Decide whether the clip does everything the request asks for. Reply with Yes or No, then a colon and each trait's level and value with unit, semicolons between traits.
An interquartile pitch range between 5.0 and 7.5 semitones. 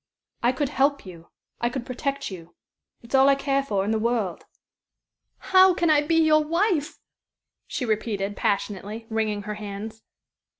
Yes: wide, 5.6 semitones